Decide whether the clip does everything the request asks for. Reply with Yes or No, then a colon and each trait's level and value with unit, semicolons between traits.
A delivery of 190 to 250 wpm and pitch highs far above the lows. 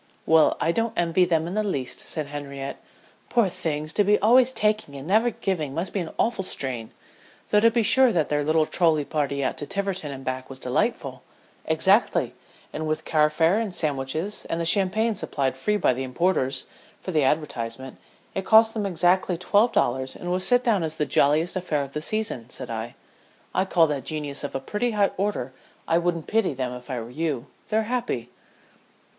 Yes: average, 195 wpm; wide, 6.3 semitones